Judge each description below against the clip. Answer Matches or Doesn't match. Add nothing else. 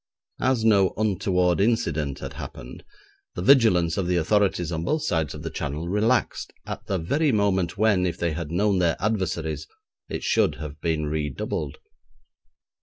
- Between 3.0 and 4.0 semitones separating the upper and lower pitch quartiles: Doesn't match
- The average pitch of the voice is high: Doesn't match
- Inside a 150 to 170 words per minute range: Matches